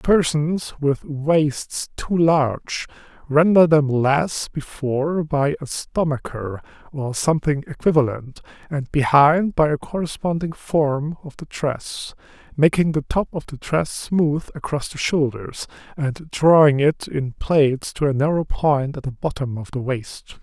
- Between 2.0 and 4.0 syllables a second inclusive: Yes, 3.9 syllables/s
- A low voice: No, medium, 145 Hz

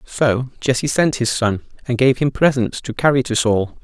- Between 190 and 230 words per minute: Yes, fast, 205 wpm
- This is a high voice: No, low, 125 Hz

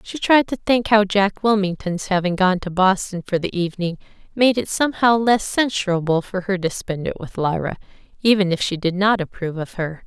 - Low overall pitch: No, high, 190 Hz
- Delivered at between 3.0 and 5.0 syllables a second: No, 5.4 syllables/s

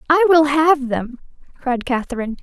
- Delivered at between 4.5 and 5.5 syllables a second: Yes, 5.1 syllables/s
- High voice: Yes, very high, 280 Hz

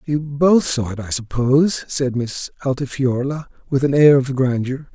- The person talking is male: Yes, male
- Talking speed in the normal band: Yes, average, 170 wpm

